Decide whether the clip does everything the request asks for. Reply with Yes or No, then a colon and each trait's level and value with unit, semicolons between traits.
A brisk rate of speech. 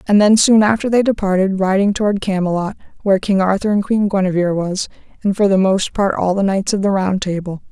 Yes: fast, 220 wpm